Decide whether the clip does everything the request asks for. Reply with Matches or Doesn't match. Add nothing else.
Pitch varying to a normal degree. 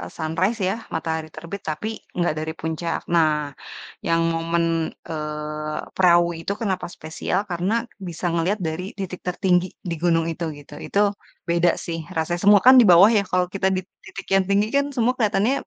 Matches